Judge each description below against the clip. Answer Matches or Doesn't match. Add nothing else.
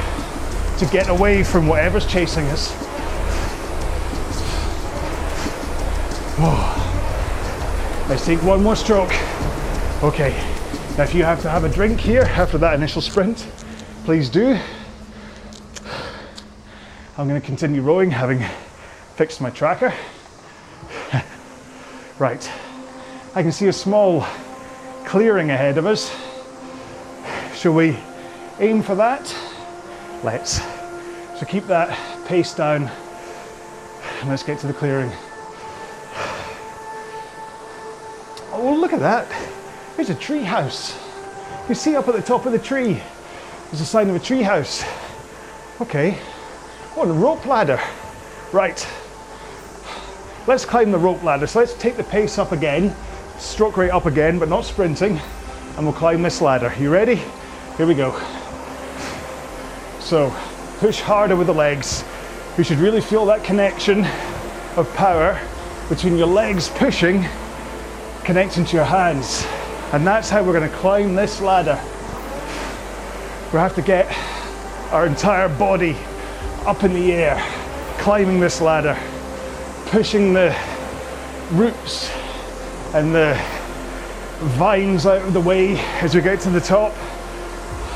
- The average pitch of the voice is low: Doesn't match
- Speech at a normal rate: Doesn't match